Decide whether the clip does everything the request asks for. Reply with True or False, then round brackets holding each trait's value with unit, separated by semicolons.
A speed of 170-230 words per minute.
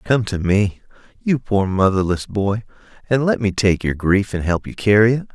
True (200 wpm)